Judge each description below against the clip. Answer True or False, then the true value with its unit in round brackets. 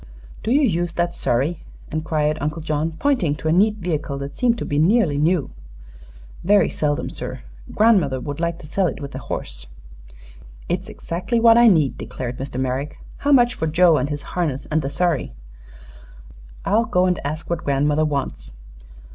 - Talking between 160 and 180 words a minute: True (175 wpm)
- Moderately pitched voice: True (155 Hz)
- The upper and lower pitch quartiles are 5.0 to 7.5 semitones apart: False (4.2 semitones)